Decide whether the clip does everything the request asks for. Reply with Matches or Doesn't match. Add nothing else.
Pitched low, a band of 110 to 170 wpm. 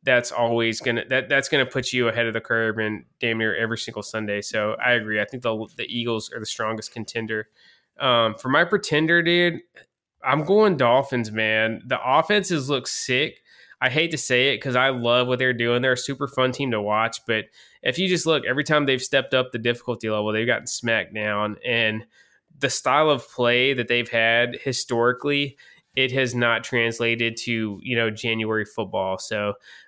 Doesn't match